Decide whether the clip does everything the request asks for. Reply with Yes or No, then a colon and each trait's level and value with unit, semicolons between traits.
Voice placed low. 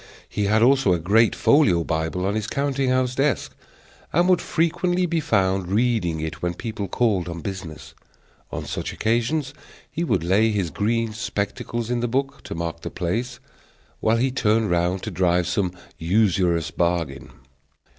Yes: low, 105 Hz